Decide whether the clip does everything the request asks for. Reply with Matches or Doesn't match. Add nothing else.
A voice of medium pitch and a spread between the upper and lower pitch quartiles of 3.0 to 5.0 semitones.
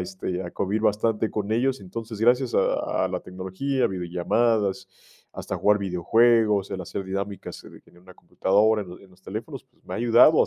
Doesn't match